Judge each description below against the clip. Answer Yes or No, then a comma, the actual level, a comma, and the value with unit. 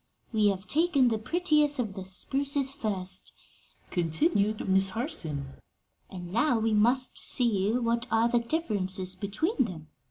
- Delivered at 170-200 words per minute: No, slow, 135 wpm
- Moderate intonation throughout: No, wide, 5.8 semitones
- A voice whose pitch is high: Yes, high, 220 Hz